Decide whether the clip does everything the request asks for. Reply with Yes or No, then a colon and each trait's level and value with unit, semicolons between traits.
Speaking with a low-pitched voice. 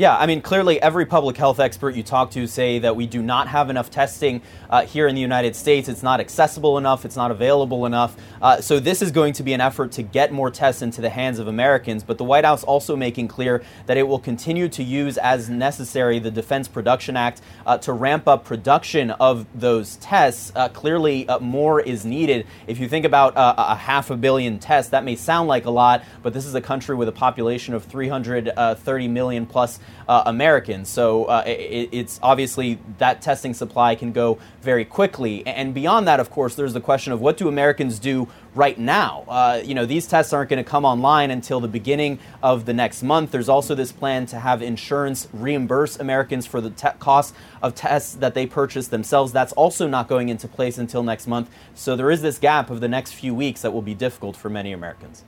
Yes: low, 125 Hz